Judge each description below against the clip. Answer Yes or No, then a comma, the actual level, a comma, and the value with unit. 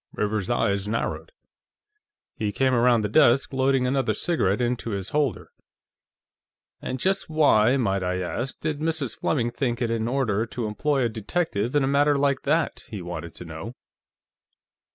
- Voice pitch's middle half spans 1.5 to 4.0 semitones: No, average, 4.7 semitones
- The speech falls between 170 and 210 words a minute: No, average, 160 wpm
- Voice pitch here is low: Yes, low, 120 Hz